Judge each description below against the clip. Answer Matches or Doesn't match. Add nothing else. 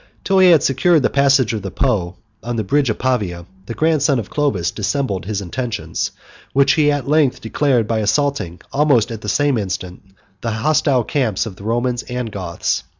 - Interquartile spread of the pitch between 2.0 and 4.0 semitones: Doesn't match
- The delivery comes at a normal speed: Matches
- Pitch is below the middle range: Matches